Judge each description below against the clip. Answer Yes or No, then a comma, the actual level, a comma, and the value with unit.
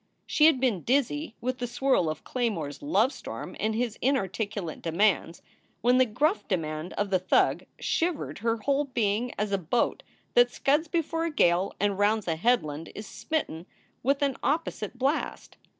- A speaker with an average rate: Yes, average, 165 wpm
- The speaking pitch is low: No, high, 235 Hz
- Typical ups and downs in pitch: No, wide, 6.2 semitones